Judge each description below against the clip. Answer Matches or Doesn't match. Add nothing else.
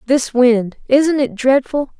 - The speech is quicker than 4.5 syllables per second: Doesn't match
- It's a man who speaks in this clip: Doesn't match